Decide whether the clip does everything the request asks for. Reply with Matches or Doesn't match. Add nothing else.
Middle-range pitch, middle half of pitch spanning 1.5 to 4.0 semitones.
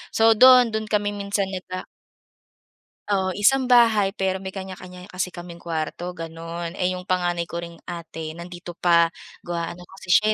Matches